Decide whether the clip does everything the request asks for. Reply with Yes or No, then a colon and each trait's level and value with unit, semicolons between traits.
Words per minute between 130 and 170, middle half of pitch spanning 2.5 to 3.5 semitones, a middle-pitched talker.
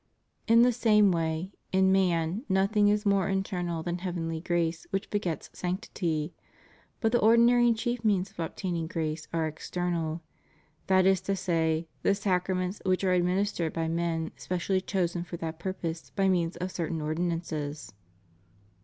Yes: average, 160 wpm; average, 2.9 semitones; medium, 180 Hz